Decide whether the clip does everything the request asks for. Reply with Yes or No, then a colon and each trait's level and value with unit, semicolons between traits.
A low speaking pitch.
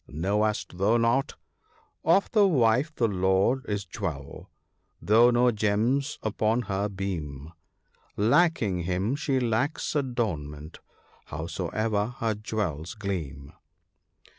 Yes: low, 105 Hz